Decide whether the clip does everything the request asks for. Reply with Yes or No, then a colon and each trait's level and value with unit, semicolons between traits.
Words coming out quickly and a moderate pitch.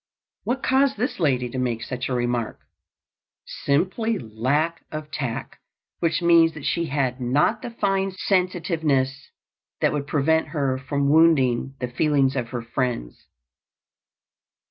No: slow, 135 wpm; medium, 145 Hz